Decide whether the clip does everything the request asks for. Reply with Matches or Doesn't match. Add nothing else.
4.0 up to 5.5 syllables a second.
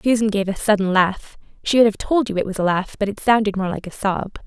Doesn't match